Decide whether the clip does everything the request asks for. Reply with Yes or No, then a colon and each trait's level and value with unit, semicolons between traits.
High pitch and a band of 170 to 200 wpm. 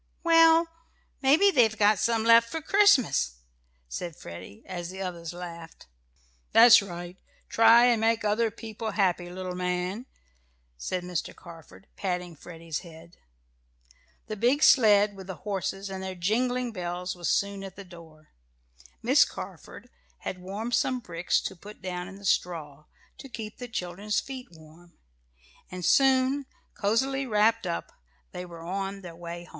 No: high, 195 Hz; average, 150 wpm